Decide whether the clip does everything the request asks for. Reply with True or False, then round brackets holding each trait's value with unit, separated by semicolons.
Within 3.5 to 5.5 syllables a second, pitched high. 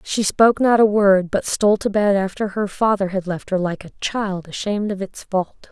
True (5.1 syllables/s; 200 Hz)